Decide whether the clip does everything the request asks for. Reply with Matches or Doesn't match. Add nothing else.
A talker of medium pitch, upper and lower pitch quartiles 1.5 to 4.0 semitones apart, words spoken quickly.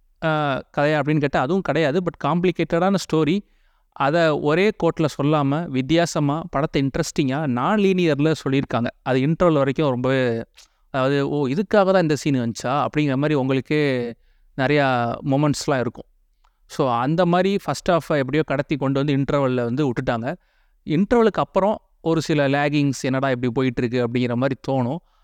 Matches